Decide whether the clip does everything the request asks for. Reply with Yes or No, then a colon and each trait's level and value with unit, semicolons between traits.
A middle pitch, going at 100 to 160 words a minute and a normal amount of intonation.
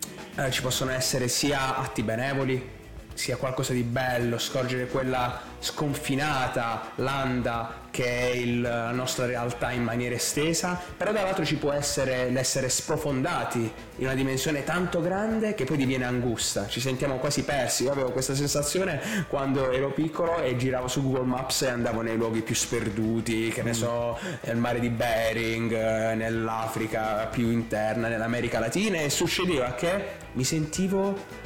No: low, 130 Hz; average, 150 wpm; average, 3.4 semitones